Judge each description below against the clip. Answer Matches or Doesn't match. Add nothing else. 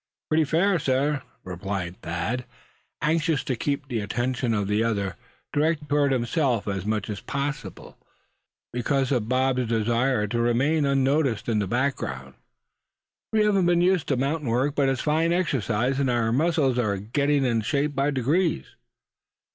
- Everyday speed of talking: Matches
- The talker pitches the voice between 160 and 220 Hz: Doesn't match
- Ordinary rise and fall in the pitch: Matches